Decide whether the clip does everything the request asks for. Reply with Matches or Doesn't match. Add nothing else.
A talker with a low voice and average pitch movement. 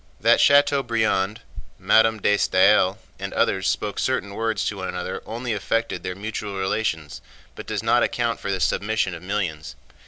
Matches